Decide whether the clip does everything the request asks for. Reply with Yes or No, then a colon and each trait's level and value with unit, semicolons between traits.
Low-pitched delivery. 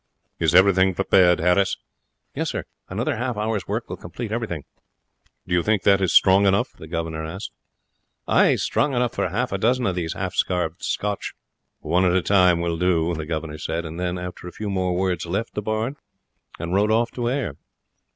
Yes: very low, 95 Hz